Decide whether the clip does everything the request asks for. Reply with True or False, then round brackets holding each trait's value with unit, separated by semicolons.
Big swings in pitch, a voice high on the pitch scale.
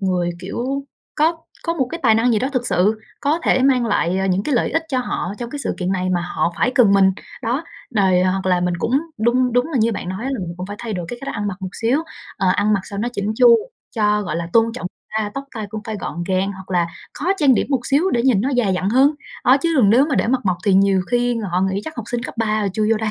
False (4.8 semitones; 220 Hz)